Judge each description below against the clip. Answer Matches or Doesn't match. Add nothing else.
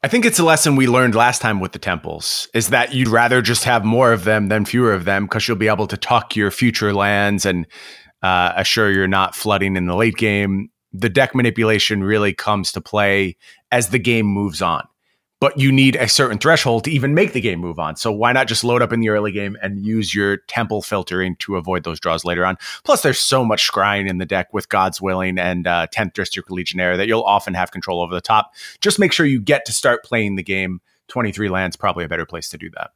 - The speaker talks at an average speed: Doesn't match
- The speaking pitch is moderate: Doesn't match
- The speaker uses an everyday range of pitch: Matches